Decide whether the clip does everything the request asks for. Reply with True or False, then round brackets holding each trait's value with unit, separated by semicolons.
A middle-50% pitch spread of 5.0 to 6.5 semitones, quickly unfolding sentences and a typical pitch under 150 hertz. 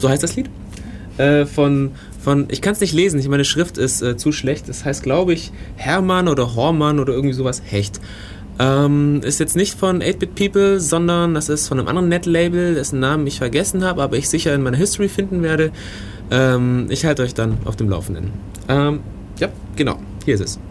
True (5.6 semitones; 205 wpm; 140 Hz)